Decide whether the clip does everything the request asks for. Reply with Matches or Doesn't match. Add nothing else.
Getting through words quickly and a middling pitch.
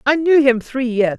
Doesn't match